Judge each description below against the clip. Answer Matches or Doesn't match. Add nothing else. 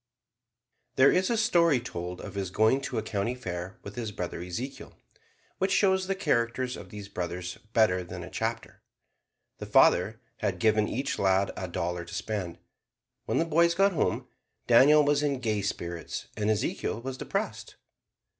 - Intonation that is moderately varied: Doesn't match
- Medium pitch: Doesn't match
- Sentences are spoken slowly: Doesn't match